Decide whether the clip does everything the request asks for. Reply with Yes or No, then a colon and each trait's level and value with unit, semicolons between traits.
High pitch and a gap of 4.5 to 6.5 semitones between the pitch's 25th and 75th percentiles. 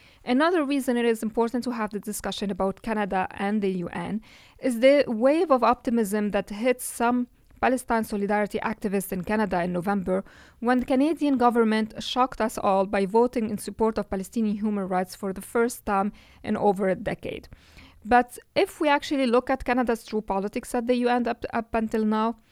No: high, 225 Hz; average, 3.3 semitones